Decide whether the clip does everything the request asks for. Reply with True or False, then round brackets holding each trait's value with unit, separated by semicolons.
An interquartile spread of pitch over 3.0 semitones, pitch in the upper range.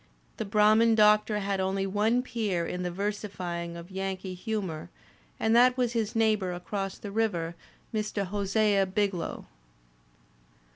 False (2.5 semitones; 200 Hz)